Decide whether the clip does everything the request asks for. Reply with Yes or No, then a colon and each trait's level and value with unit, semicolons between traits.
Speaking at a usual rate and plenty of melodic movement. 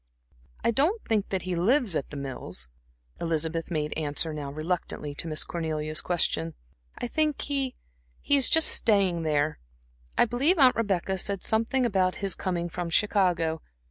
Yes: average, 155 wpm; wide, 6.5 semitones